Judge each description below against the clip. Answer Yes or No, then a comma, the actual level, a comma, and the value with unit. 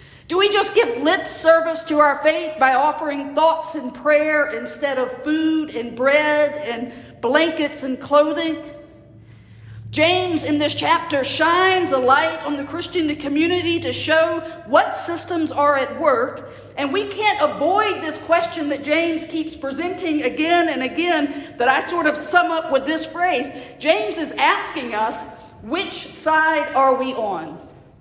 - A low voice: No, very high, 310 Hz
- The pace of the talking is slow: No, average, 155 wpm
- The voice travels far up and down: No, narrow, 2.6 semitones